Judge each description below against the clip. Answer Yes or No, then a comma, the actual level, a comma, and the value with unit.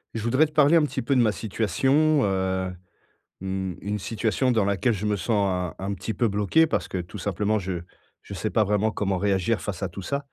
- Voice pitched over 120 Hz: No, low, 105 Hz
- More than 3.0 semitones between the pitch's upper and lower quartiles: Yes, average, 3.6 semitones